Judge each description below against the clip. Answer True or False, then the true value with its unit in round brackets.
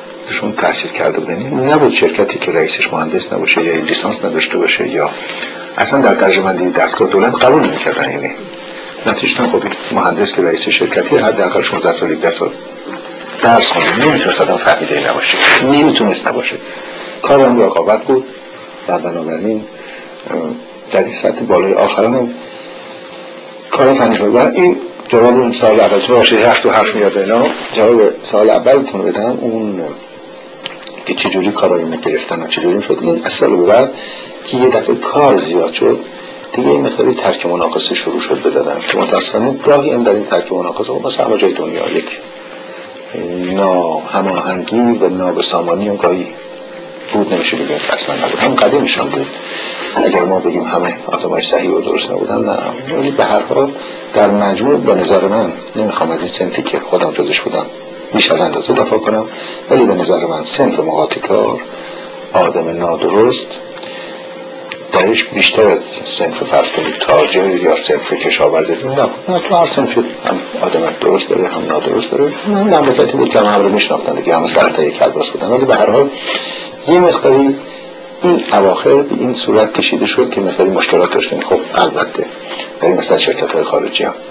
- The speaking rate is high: True (165 wpm)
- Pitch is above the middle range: True (360 Hz)